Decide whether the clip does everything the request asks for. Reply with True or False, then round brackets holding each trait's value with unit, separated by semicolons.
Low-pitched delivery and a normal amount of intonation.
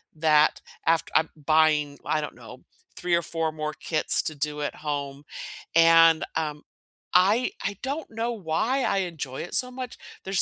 False (160 Hz; 4.1 semitones)